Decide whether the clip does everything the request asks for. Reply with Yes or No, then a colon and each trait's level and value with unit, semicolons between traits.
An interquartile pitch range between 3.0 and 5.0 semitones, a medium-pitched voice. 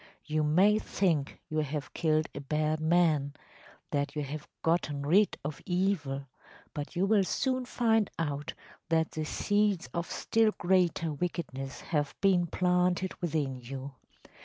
Yes: average, 3.9 semitones; medium, 160 Hz